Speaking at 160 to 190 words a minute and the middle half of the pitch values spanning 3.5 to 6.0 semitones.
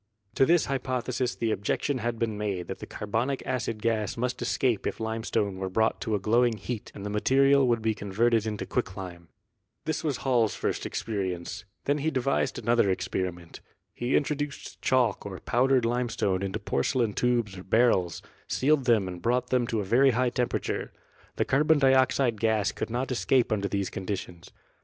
Yes: average, 180 wpm; average, 4.0 semitones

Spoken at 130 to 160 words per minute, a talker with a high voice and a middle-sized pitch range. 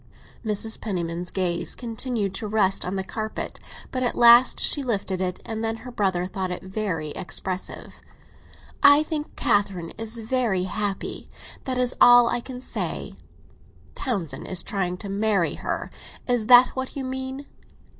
Yes: average, 150 wpm; high, 215 Hz; average, 4.6 semitones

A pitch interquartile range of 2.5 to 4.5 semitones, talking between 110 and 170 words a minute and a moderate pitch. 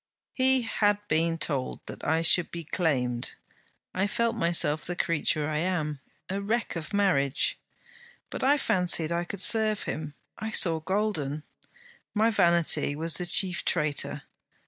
No: average, 5.0 semitones; average, 145 wpm; medium, 170 Hz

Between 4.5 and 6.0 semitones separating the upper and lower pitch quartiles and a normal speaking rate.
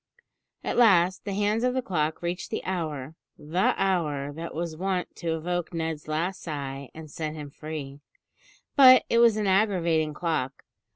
No: average, 3.8 semitones; average, 165 wpm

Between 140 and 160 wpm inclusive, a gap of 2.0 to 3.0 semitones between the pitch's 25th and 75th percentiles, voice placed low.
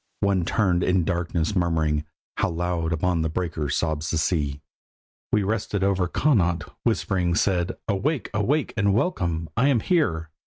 No: average, 150 wpm; average, 3.7 semitones; very low, 90 Hz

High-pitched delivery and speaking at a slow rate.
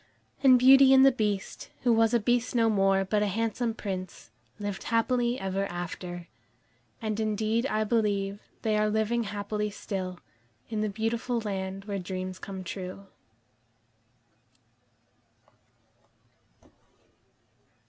Yes: high, 210 Hz; slow, 120 wpm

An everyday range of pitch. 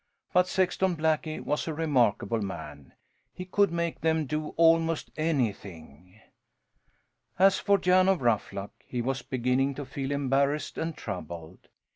No: wide, 6.4 semitones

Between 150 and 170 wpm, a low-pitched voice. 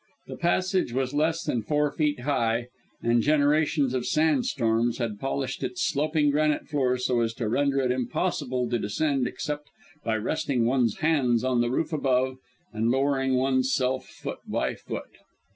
Yes: average, 165 wpm; low, 130 Hz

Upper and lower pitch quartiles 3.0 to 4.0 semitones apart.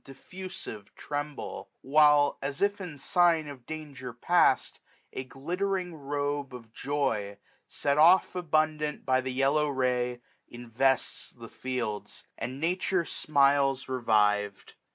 Yes: average, 3.4 semitones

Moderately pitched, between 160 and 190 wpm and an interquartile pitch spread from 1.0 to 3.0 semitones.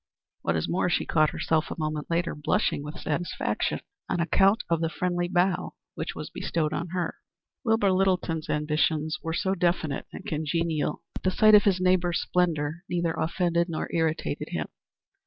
Yes: medium, 170 Hz; average, 170 wpm; narrow, 2.6 semitones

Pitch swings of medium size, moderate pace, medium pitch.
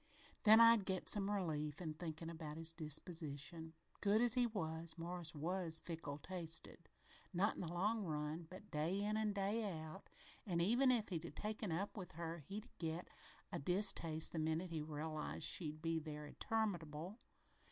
Yes: average, 4.0 semitones; average, 170 wpm; medium, 170 Hz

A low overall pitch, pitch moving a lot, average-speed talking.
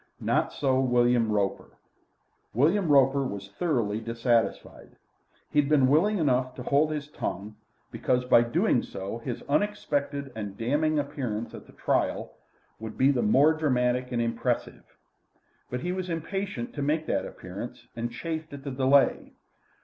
No: low, 130 Hz; average, 4.1 semitones; average, 150 wpm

